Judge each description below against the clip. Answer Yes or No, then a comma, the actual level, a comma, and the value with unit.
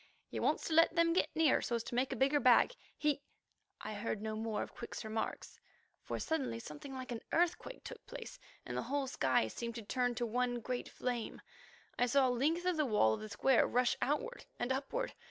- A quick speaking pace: Yes, fast, 215 wpm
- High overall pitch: Yes, very high, 250 Hz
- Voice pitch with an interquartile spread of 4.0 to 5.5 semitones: Yes, average, 4.7 semitones